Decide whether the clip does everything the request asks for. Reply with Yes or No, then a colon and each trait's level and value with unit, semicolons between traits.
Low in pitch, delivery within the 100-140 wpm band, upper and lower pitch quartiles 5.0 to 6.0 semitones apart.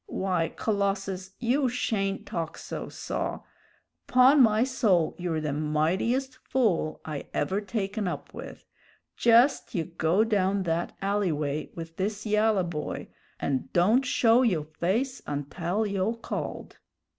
No: high, 195 Hz; slow, 135 wpm; average, 5.3 semitones